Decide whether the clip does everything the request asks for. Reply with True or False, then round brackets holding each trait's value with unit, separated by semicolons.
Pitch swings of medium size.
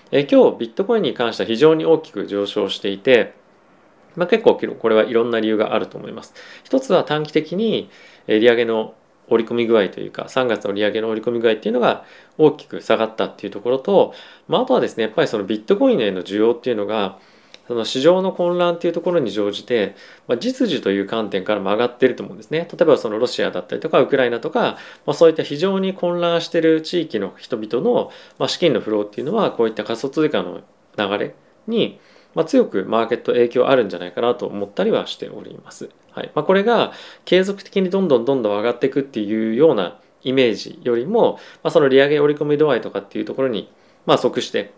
False (7.8 semitones)